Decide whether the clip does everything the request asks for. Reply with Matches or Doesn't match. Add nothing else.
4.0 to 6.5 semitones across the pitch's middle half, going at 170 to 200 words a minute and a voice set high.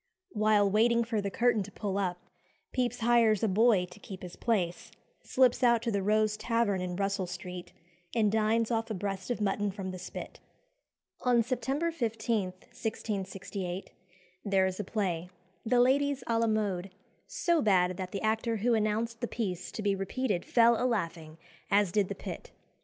Doesn't match